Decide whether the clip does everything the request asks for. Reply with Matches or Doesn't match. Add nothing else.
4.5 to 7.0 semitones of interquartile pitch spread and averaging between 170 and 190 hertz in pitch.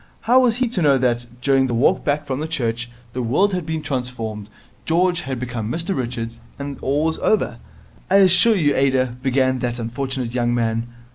Doesn't match